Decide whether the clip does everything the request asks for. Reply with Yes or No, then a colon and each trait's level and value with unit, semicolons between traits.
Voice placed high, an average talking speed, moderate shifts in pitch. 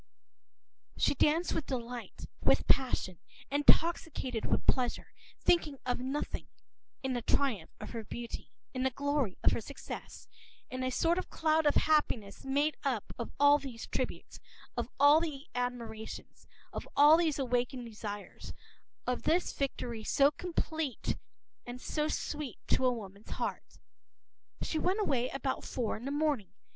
Yes: very high, 265 Hz; average, 150 wpm; average, 3.8 semitones